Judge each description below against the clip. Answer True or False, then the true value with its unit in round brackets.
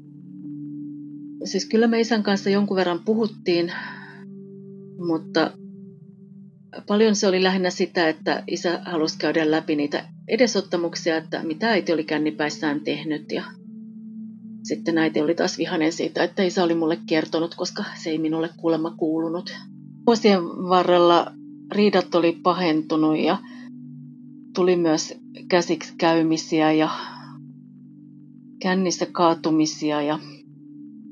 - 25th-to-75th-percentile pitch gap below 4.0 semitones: True (3.6 semitones)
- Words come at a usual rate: True (115 wpm)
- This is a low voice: False (175 Hz)